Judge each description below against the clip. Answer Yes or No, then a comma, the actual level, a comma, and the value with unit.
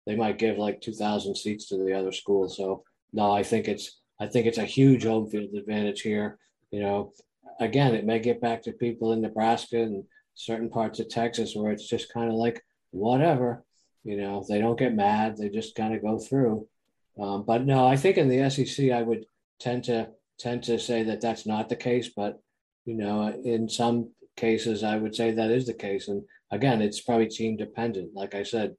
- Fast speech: Yes, fast, 215 wpm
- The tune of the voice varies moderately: No, narrow, 2.0 semitones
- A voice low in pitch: Yes, low, 115 Hz